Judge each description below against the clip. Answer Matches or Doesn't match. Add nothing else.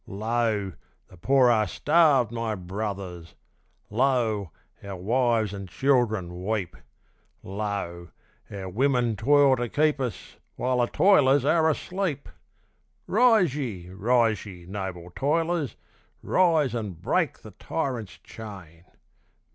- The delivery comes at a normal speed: Doesn't match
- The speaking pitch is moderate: Doesn't match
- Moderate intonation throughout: Doesn't match